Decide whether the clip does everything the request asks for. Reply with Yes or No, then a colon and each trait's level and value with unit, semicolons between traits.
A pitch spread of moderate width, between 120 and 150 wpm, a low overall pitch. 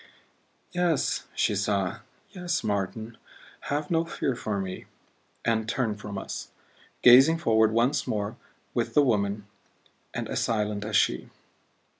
Yes: average, 4.4 semitones; slow, 135 wpm; low, 110 Hz